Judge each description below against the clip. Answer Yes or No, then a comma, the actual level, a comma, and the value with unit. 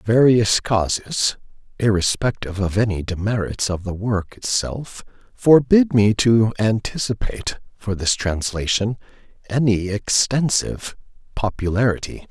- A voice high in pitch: No, low, 105 Hz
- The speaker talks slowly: Yes, slow, 100 wpm